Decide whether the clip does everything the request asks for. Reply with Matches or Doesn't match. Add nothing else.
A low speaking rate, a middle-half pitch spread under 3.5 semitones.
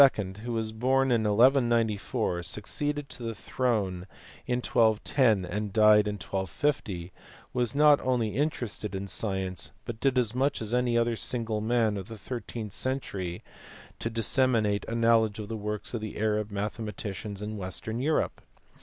Doesn't match